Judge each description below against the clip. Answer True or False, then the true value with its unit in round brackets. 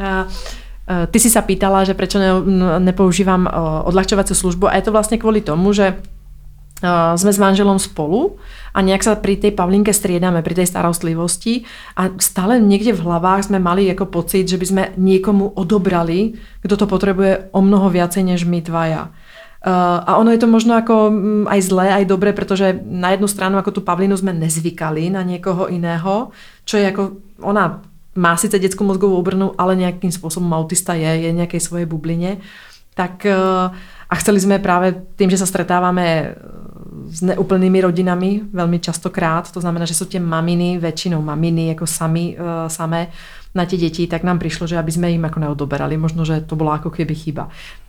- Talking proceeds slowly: False (170 wpm)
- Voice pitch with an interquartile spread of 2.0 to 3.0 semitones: True (2.4 semitones)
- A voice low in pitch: False (185 Hz)